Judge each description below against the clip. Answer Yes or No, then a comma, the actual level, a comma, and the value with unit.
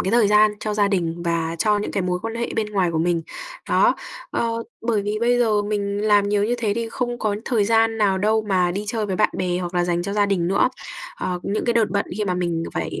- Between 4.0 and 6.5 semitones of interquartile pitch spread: No, average, 3.4 semitones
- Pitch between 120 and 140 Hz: No, high, 205 Hz